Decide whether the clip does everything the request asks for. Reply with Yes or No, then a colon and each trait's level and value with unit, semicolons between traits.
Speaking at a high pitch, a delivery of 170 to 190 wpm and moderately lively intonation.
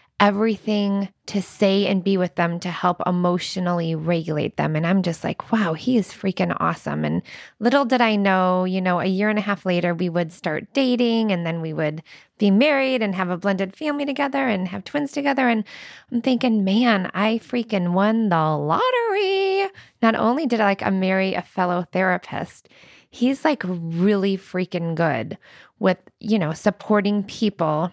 Yes: high, 195 Hz; average, 175 wpm; average, 4.2 semitones